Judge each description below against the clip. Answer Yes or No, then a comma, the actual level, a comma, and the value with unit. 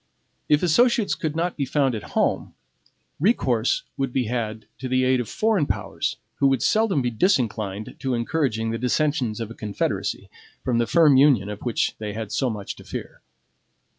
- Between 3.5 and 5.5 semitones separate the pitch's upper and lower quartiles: Yes, average, 5.1 semitones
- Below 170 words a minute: No, average, 180 wpm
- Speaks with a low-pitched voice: Yes, low, 125 Hz